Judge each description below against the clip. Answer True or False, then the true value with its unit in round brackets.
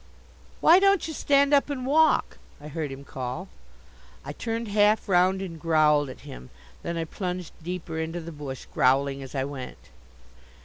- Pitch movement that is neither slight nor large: False (7.0 semitones)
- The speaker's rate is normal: True (170 wpm)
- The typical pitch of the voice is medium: True (170 Hz)